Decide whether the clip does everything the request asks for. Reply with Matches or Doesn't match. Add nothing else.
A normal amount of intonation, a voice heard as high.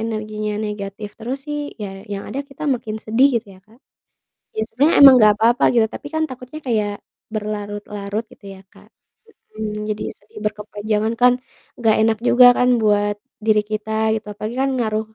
Doesn't match